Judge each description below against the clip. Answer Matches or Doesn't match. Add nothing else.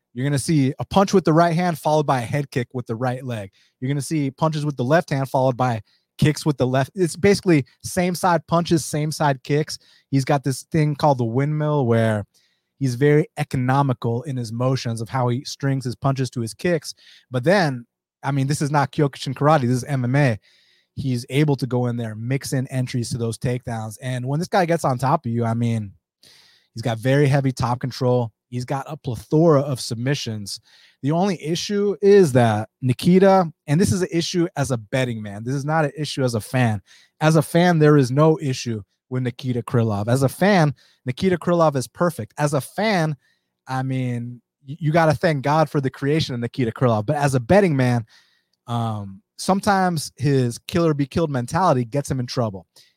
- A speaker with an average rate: Doesn't match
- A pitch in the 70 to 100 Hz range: Doesn't match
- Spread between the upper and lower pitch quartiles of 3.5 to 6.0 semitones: Matches